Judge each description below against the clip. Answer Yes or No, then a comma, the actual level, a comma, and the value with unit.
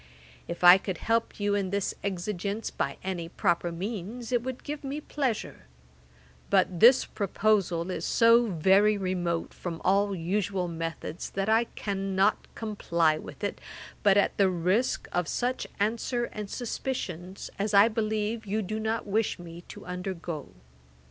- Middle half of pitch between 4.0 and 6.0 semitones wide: No, average, 3.6 semitones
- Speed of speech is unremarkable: Yes, average, 150 wpm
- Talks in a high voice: Yes, high, 200 Hz